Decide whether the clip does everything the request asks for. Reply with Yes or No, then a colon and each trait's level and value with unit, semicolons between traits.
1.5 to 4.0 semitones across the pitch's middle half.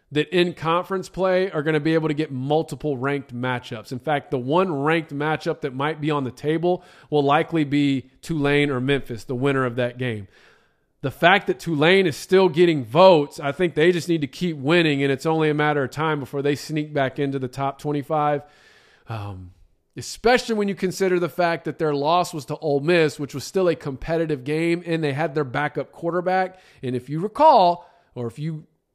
Yes: average, 3.5 semitones